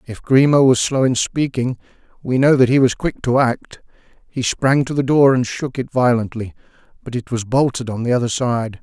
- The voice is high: No, low, 125 Hz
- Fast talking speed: Yes, fast, 210 wpm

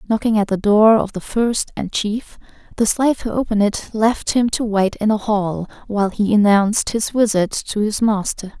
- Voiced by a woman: Yes, female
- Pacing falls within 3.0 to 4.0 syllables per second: No, 4.9 syllables/s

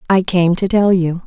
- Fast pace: Yes, fast, 235 wpm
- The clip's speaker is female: Yes, female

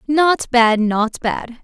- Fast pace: No, average, 145 wpm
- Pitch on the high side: Yes, very high, 250 Hz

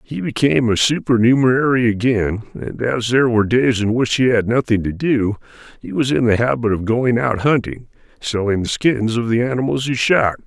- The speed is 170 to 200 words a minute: Yes, average, 195 wpm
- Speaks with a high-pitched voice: No, low, 120 Hz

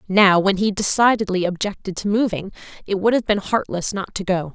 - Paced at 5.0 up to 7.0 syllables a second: Yes, 5.4 syllables/s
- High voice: Yes, high, 195 Hz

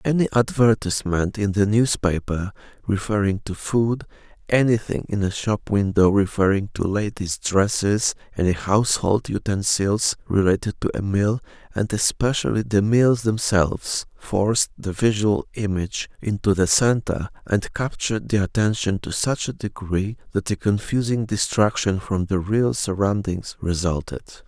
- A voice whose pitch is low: Yes, low, 105 Hz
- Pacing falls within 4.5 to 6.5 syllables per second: Yes, 4.6 syllables/s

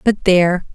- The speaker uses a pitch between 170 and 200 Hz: Yes, medium, 185 Hz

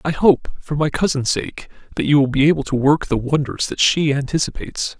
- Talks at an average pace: No, fast, 215 wpm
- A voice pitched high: No, medium, 150 Hz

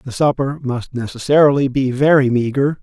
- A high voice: No, low, 135 Hz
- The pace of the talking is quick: No, average, 150 wpm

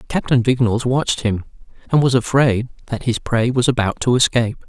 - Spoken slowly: No, average, 180 wpm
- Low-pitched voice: Yes, low, 120 Hz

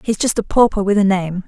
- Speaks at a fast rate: Yes, fast, 285 wpm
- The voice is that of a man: No, female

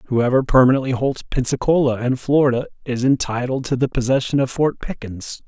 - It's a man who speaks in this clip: Yes, male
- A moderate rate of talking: Yes, average, 155 wpm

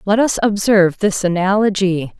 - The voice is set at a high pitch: Yes, high, 195 Hz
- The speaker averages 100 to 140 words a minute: Yes, slow, 135 wpm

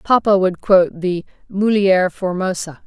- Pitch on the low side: No, medium, 185 Hz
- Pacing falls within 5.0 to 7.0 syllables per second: No, 4.4 syllables/s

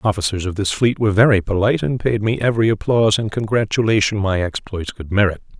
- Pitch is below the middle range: Yes, low, 105 Hz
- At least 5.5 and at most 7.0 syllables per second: Yes, 6.5 syllables/s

